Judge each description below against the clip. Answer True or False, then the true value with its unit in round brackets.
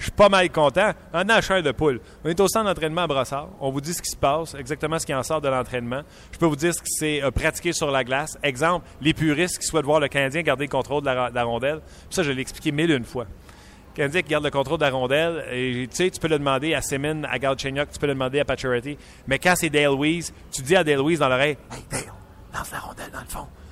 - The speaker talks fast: True (280 wpm)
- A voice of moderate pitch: True (145 Hz)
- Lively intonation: False (3.5 semitones)